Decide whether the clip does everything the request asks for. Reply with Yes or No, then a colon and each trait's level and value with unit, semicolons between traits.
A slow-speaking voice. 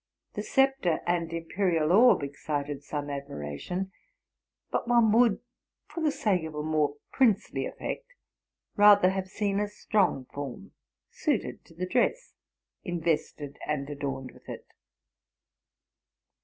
Yes: slow, 130 wpm